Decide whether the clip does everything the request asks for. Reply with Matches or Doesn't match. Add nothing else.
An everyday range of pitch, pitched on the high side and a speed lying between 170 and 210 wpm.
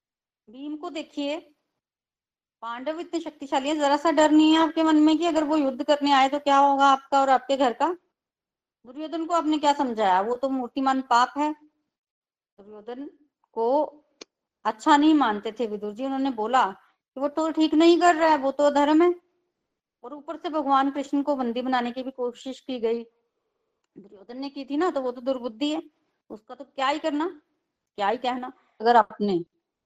Matches